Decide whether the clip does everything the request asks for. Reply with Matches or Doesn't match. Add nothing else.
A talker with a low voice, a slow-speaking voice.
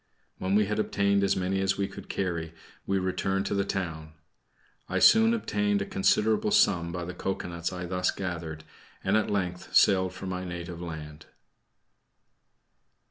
Doesn't match